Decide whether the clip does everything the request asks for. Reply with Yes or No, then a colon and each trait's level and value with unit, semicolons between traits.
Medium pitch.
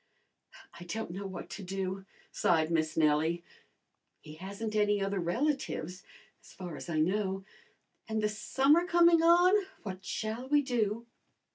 No: high, 200 Hz